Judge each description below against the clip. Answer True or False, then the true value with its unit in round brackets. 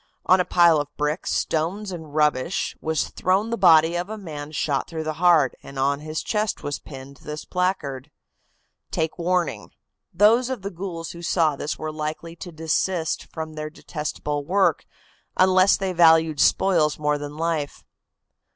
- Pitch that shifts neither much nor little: True (3.3 semitones)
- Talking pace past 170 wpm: False (165 wpm)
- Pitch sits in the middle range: True (160 Hz)